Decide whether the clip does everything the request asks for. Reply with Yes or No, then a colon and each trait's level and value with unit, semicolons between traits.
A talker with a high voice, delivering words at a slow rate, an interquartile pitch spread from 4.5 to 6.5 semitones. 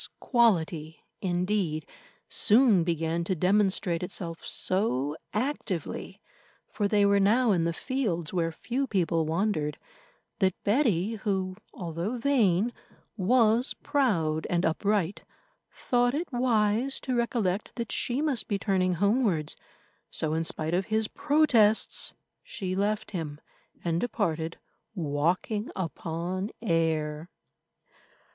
Yes: high, 195 Hz; slow, 115 wpm; average, 5.2 semitones